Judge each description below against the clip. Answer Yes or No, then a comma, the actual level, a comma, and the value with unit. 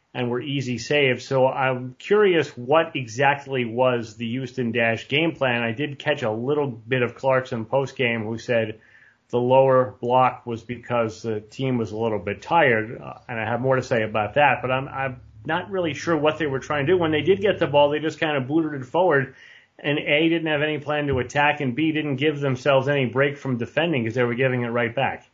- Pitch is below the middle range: Yes, low, 130 Hz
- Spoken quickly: Yes, fast, 230 wpm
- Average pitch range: Yes, average, 3.4 semitones